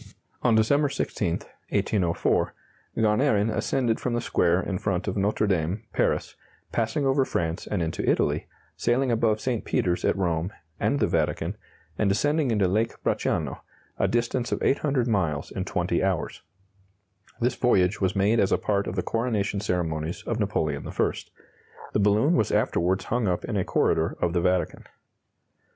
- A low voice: Yes, low, 105 Hz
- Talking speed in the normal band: Yes, average, 160 wpm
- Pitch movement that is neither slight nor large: Yes, average, 4.6 semitones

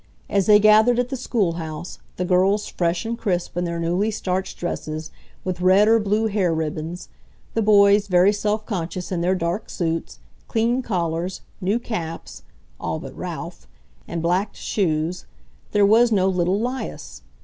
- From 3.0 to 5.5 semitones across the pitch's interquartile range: Yes, average, 3.8 semitones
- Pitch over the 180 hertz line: Yes, high, 190 Hz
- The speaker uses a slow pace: No, average, 160 wpm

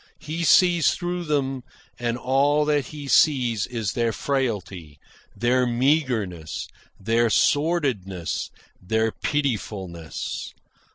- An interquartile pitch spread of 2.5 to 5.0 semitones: No, wide, 5.4 semitones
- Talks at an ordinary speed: No, slow, 100 wpm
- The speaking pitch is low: Yes, low, 125 Hz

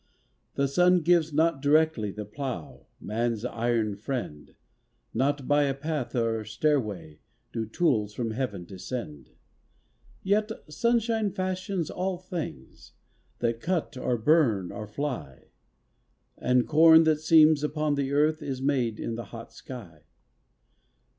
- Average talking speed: No, slow, 125 wpm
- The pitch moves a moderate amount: No, wide, 6.0 semitones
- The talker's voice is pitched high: No, low, 135 Hz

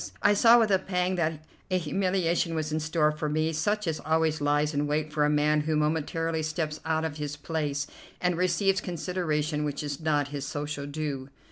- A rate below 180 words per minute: No, average, 200 wpm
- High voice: No, medium, 155 Hz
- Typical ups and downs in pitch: No, narrow, 2.2 semitones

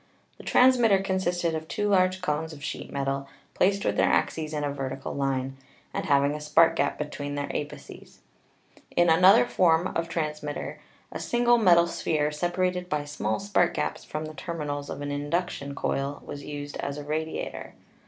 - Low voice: No, medium, 155 Hz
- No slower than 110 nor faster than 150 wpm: No, average, 175 wpm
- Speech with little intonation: No, average, 3.8 semitones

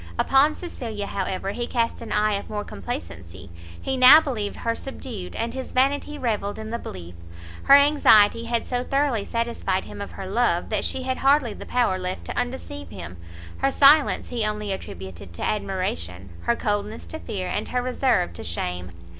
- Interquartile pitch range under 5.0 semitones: No, wide, 5.4 semitones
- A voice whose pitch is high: Yes, high, 220 Hz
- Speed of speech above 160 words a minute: Yes, average, 180 wpm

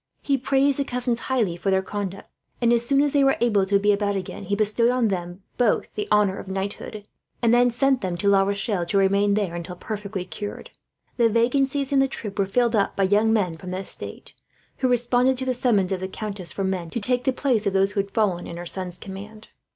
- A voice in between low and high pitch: No, high, 205 Hz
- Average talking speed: No, fast, 235 wpm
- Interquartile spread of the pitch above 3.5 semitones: Yes, average, 4.1 semitones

